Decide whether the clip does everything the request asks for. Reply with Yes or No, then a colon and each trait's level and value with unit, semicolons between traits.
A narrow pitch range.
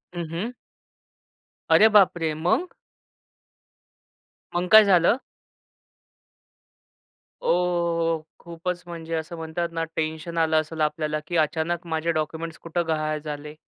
Yes: narrow, 1.5 semitones